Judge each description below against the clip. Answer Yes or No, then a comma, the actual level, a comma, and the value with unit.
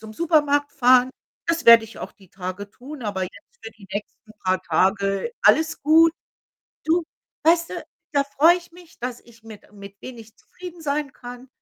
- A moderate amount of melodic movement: No, wide, 7.1 semitones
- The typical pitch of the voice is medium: No, very high, 250 Hz